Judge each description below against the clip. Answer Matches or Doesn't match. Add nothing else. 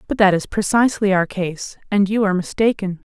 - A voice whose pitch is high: Matches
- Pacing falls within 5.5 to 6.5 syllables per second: Matches